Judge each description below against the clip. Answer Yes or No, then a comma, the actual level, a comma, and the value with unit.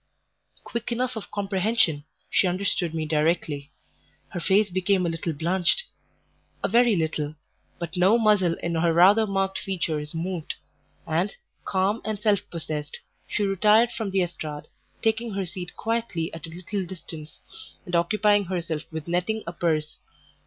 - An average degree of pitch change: Yes, average, 3.9 semitones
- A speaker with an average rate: Yes, average, 150 wpm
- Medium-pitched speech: Yes, medium, 180 Hz